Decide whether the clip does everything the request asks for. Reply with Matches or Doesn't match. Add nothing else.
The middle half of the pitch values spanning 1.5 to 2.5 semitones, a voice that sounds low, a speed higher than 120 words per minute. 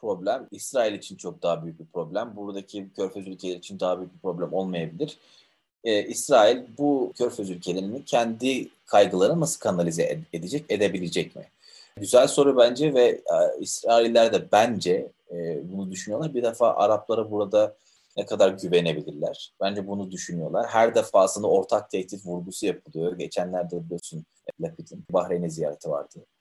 Doesn't match